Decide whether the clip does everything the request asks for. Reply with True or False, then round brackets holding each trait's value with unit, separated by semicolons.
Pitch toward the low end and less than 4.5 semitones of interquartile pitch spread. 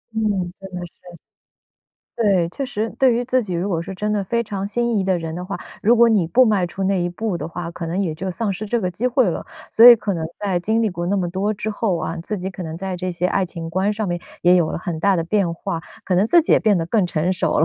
False (190 Hz; 3.5 semitones)